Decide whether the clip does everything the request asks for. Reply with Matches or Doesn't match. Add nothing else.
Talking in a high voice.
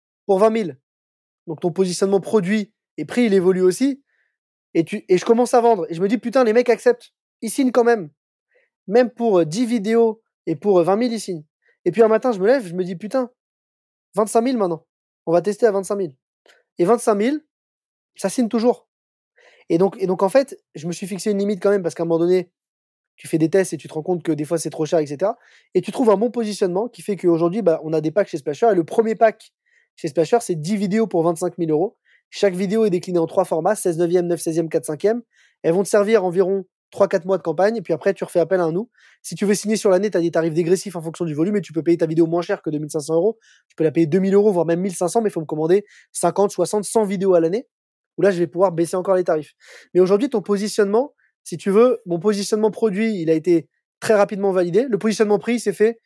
Matches